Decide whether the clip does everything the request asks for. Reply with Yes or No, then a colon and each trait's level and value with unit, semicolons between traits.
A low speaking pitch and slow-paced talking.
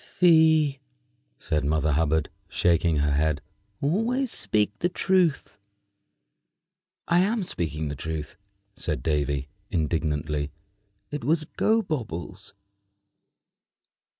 Yes: very low, 85 Hz; slow, 95 wpm